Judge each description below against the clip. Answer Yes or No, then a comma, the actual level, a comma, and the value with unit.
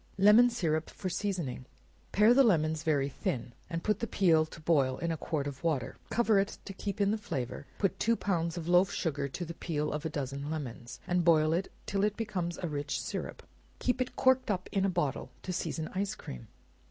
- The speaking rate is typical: No, fast, 215 wpm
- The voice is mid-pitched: Yes, medium, 170 Hz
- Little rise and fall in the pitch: No, average, 5.0 semitones